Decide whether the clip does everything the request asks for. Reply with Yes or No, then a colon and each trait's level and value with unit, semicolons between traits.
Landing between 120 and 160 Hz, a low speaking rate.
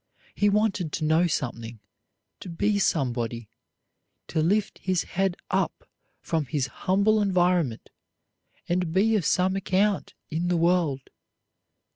No: medium, 175 Hz; slow, 125 wpm